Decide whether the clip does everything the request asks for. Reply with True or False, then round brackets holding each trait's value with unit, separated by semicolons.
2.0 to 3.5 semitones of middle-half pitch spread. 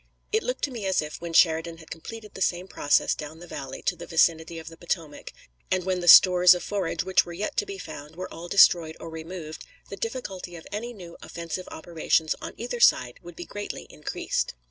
True (2.9 semitones)